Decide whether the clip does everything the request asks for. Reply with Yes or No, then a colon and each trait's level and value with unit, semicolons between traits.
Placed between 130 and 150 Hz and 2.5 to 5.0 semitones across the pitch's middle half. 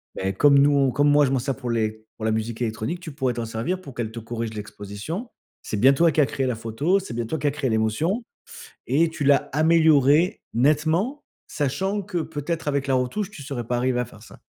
No: medium, 140 Hz; wide, 5.5 semitones